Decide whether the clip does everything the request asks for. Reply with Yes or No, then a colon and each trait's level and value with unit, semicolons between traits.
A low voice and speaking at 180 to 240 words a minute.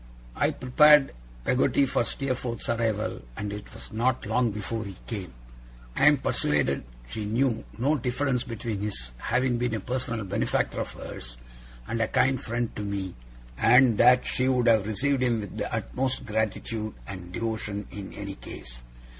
No: low, 115 Hz; average, 165 wpm